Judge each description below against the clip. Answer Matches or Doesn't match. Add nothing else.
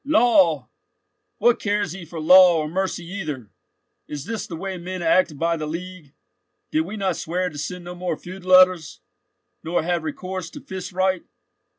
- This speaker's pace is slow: Doesn't match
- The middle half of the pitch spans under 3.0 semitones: Matches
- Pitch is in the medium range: Matches